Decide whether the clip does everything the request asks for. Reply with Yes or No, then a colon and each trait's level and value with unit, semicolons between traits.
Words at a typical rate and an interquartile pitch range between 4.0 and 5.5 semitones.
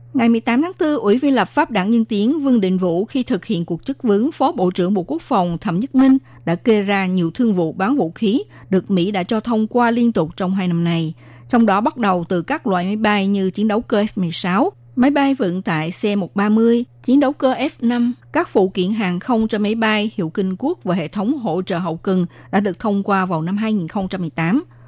Yes: average, 235 wpm; average, 4.6 semitones